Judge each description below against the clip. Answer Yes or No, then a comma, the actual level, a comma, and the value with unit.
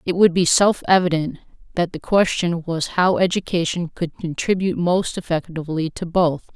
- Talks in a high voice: No, medium, 170 Hz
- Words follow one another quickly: No, average, 155 wpm